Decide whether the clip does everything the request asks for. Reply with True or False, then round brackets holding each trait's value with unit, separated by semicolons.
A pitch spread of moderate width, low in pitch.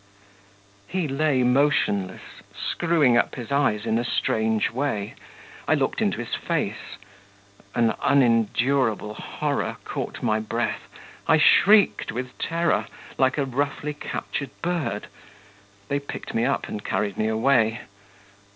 True (4.4 semitones; 125 Hz)